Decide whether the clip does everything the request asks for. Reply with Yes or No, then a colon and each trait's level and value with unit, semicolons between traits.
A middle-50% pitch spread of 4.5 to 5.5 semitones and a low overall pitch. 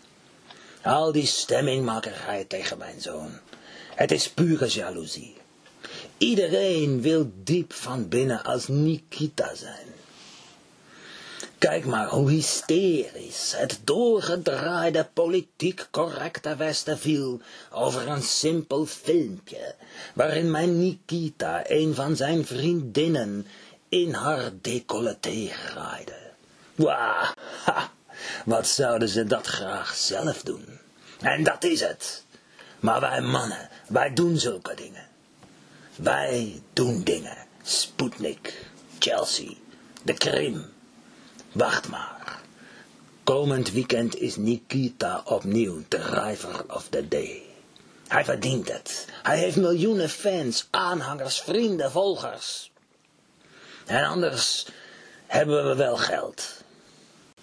No: average, 5.1 semitones; medium, 155 Hz